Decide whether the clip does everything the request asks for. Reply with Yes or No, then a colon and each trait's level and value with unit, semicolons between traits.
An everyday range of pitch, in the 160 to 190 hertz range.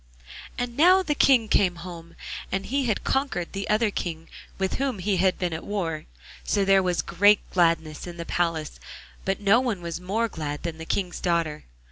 Yes: average, 4.0 semitones; medium, 185 Hz